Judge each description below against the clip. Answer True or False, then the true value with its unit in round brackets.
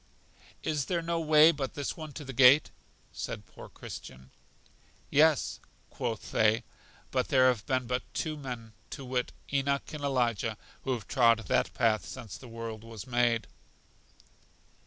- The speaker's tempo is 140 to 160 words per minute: True (155 wpm)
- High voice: False (125 Hz)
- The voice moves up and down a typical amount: True (3.7 semitones)